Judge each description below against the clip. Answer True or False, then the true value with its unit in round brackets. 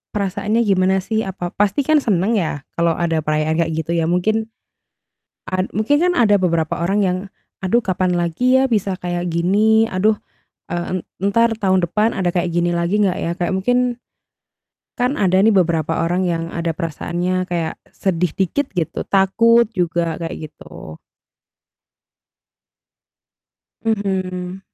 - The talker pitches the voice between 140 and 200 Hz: True (185 Hz)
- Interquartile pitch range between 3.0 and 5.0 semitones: True (3.5 semitones)